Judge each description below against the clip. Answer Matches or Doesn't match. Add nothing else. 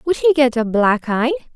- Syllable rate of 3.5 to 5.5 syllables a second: Matches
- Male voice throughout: Doesn't match